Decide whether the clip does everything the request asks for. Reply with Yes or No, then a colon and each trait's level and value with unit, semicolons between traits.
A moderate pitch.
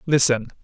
No: low, 130 Hz